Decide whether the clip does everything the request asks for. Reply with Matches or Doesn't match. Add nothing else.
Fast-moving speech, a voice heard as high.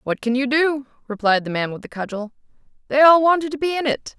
Matches